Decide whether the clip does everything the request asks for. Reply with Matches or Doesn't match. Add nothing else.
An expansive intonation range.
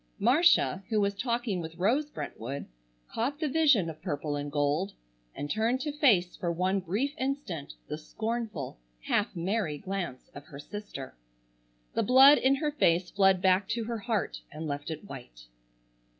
Matches